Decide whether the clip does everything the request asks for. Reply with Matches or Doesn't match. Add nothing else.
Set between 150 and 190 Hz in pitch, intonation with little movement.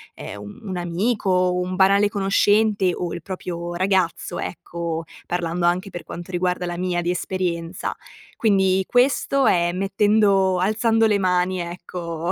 Matches